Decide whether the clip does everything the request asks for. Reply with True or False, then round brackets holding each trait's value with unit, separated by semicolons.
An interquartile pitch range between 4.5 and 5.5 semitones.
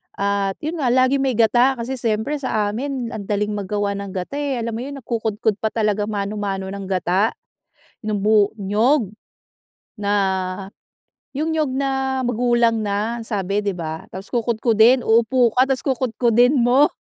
False (4.0 semitones)